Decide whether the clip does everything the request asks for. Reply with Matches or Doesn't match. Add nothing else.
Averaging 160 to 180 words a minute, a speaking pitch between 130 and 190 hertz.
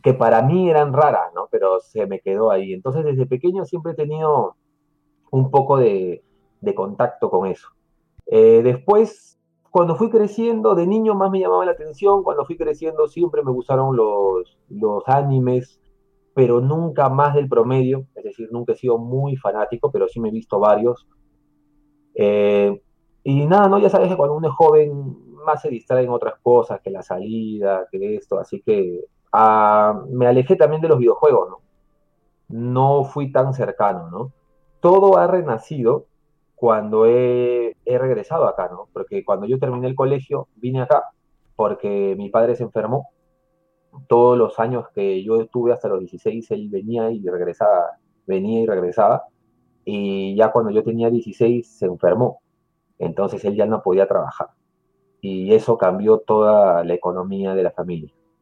Matches